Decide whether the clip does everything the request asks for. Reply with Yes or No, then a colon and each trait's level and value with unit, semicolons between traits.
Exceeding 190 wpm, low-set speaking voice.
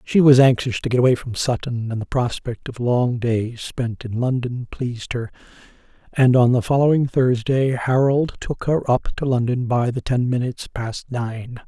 No: average, 185 wpm; low, 125 Hz